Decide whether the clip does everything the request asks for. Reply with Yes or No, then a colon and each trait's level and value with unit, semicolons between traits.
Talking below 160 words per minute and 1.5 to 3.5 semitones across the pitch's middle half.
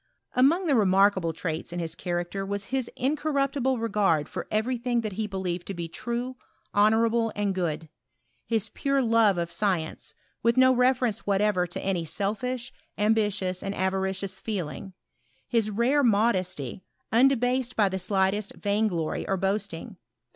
No: average, 145 wpm; average, 4.1 semitones